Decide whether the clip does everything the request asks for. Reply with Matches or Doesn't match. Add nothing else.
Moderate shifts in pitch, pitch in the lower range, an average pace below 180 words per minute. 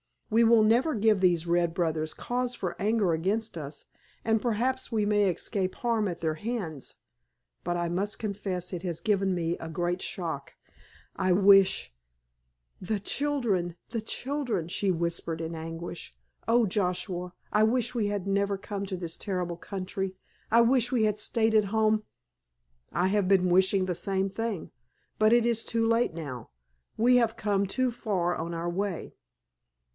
Doesn't match